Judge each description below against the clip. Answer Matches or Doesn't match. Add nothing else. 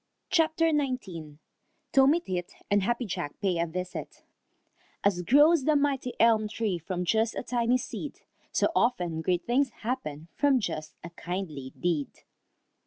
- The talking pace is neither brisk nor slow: Matches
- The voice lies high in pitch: Matches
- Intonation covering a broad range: Matches